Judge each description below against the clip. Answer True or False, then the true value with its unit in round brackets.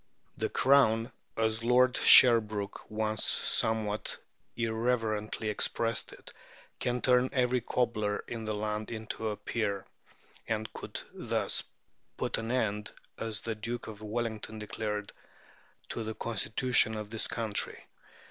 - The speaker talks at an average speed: False (125 wpm)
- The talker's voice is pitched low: True (110 Hz)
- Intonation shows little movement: True (1.6 semitones)